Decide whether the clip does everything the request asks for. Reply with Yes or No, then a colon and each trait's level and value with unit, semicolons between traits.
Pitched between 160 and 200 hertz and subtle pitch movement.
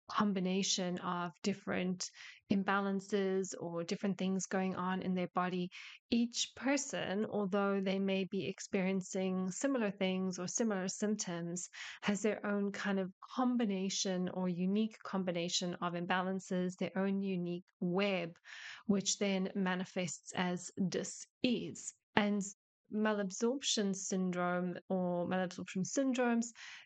Yes: high, 190 Hz; narrow, 2.0 semitones